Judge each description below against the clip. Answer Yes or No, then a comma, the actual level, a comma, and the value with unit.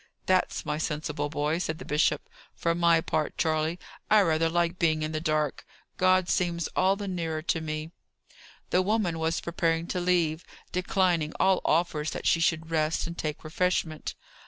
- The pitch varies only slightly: Yes, narrow, 2.2 semitones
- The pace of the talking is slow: No, average, 170 wpm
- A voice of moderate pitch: Yes, medium, 165 Hz